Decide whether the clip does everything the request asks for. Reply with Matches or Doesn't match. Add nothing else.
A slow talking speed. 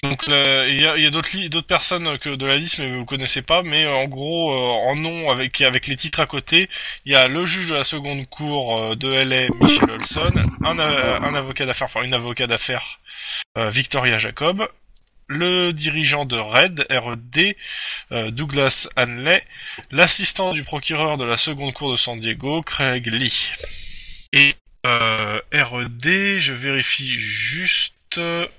Doesn't match